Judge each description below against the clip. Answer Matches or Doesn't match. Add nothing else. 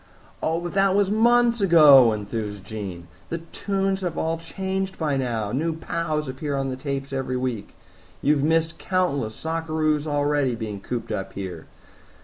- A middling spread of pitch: Doesn't match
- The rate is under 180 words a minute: Matches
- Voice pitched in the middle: Matches